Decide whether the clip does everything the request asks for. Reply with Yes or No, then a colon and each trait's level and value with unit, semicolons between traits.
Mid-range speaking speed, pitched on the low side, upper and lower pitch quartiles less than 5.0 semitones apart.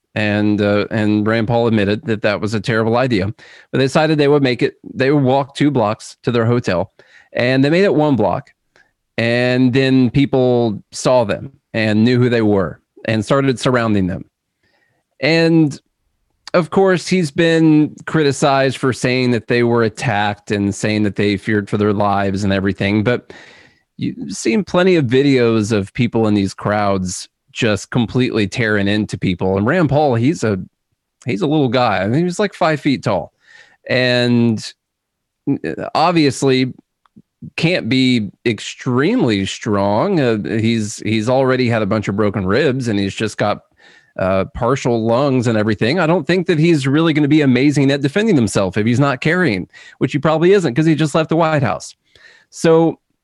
No: average, 175 wpm; low, 120 Hz; average, 5.3 semitones